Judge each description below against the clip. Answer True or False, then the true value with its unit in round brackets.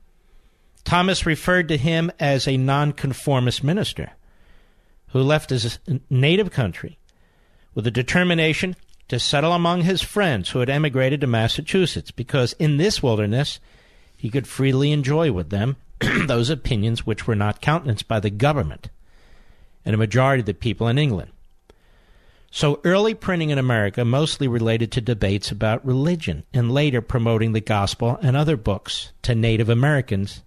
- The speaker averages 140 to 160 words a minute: True (150 wpm)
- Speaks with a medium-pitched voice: False (130 Hz)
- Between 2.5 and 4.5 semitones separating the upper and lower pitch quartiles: False (5.2 semitones)